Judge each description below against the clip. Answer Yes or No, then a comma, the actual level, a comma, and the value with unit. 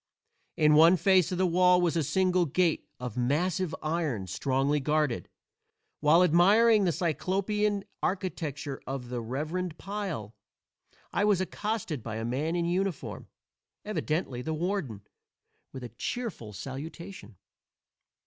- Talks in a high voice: No, medium, 165 Hz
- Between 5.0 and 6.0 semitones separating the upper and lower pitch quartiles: Yes, wide, 5.6 semitones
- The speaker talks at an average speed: No, slow, 130 wpm